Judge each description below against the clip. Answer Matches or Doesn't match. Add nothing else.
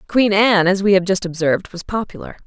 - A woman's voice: Matches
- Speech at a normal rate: Doesn't match